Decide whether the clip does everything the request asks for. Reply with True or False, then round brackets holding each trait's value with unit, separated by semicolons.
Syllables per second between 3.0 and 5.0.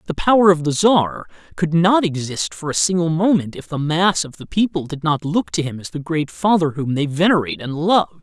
False (5.3 syllables/s)